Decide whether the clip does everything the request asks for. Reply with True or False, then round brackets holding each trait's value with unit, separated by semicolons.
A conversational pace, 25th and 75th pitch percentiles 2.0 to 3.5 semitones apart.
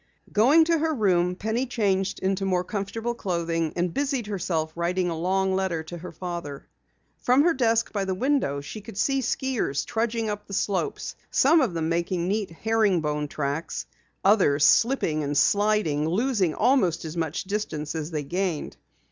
False (170 wpm; 5.3 semitones)